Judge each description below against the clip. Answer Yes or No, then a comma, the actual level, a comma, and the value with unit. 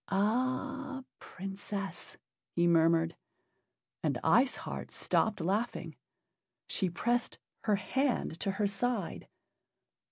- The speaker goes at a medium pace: No, slow, 95 wpm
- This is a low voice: No, high, 205 Hz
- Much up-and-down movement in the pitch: No, average, 4.6 semitones